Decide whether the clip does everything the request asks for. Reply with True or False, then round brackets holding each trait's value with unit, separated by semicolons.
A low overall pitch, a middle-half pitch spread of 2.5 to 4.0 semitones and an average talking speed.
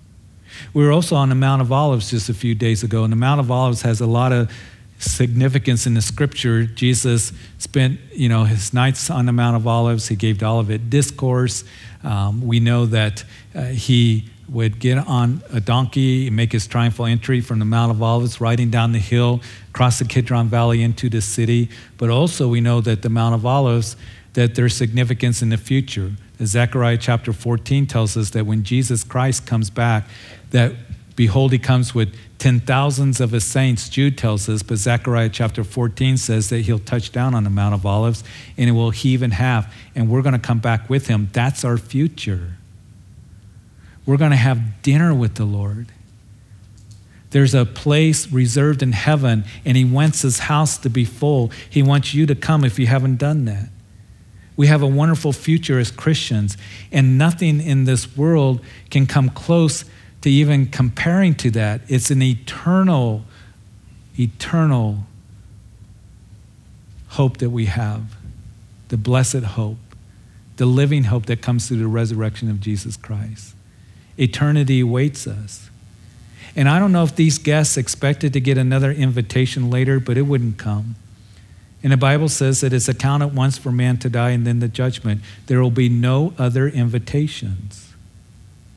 True (120 Hz; 3.2 semitones; 175 wpm)